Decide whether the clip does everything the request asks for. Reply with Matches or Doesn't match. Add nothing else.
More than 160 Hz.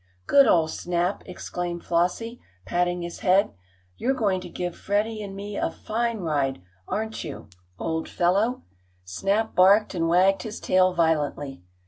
Matches